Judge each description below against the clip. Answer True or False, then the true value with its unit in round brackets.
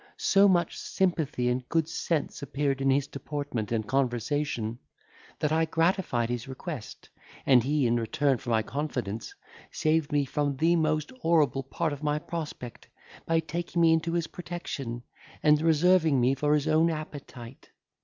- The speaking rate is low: False (155 wpm)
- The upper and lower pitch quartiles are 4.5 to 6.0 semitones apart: False (4.1 semitones)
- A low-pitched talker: False (145 Hz)